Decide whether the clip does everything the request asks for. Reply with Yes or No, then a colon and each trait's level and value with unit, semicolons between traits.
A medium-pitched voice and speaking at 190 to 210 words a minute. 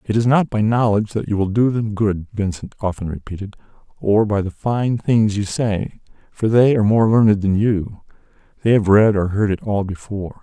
No: low, 105 Hz; average, 200 wpm